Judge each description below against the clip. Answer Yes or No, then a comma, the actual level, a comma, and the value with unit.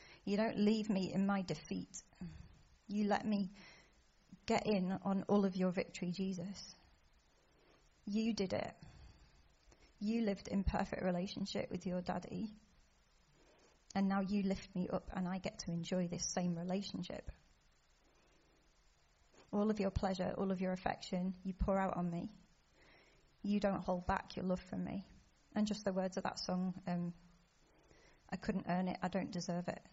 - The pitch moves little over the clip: Yes, narrow, 2.2 semitones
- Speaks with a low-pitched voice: No, high, 190 Hz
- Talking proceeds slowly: No, average, 160 wpm